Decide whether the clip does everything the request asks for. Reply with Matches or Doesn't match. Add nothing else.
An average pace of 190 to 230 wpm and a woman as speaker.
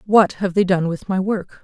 Doesn't match